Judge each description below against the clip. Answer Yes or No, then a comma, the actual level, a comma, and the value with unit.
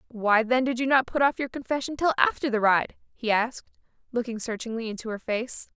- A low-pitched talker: No, high, 240 Hz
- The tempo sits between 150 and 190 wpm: No, fast, 205 wpm